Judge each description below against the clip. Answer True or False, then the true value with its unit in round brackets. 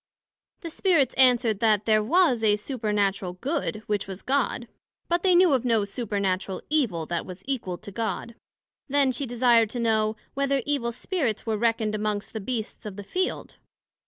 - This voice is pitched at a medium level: False (230 Hz)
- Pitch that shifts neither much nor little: True (4.3 semitones)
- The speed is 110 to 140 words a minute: False (170 wpm)